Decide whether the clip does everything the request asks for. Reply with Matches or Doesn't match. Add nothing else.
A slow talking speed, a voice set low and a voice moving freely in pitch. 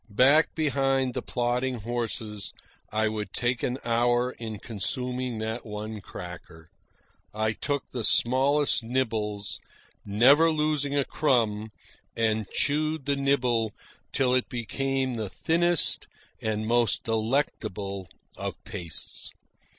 Doesn't match